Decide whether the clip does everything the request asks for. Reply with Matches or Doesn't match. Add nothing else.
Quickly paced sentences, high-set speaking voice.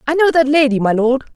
Matches